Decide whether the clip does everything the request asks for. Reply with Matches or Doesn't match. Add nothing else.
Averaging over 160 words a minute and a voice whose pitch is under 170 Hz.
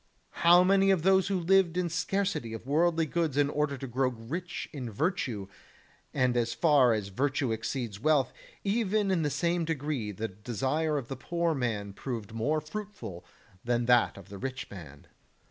Matches